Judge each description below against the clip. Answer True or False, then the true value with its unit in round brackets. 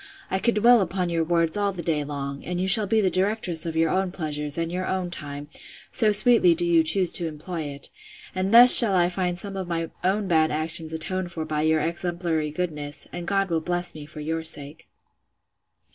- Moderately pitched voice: True (170 Hz)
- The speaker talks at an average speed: False (215 wpm)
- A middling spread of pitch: True (3.0 semitones)